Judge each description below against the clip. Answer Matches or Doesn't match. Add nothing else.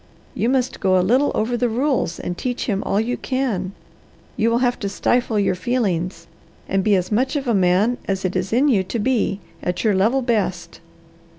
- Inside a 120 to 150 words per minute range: Doesn't match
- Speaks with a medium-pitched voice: Doesn't match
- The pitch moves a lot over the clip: Doesn't match